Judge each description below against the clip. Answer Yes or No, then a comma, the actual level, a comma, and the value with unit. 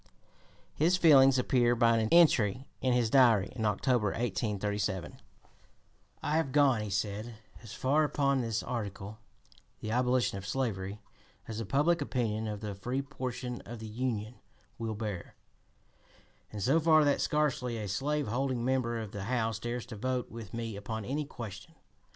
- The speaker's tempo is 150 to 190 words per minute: Yes, average, 160 wpm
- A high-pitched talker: No, low, 120 Hz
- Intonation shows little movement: No, average, 3.7 semitones